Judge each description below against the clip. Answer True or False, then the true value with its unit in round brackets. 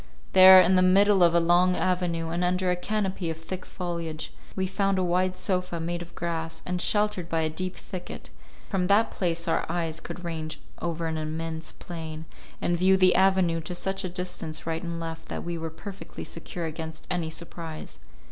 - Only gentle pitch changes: True (2.1 semitones)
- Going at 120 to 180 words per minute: False (195 wpm)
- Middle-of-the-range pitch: True (175 Hz)